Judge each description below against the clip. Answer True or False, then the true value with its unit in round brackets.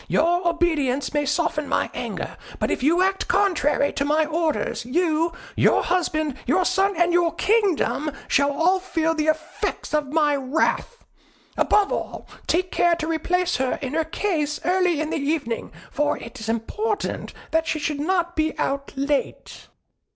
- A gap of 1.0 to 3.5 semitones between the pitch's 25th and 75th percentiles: True (3.2 semitones)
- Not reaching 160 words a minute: False (165 wpm)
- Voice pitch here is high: True (320 Hz)